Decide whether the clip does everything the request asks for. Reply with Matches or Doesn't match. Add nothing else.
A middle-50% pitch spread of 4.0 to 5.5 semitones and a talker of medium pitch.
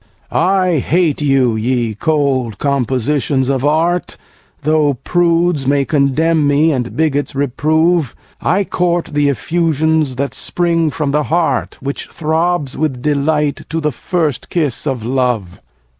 Doesn't match